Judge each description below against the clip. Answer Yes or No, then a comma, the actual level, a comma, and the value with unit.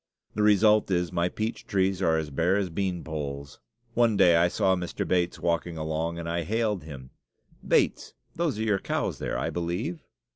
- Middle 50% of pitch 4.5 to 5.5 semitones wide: No, average, 3.8 semitones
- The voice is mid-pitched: No, very low, 90 Hz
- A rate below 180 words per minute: No, average, 185 wpm